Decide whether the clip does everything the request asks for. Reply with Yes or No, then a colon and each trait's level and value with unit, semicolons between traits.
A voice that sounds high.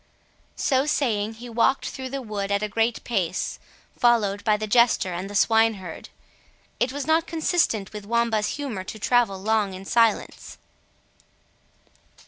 Yes: high, 225 Hz